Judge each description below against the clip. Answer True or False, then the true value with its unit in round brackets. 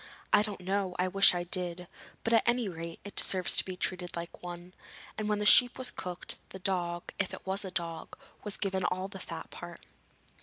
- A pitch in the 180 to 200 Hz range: True (185 Hz)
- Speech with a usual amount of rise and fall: False (2.3 semitones)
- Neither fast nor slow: False (215 wpm)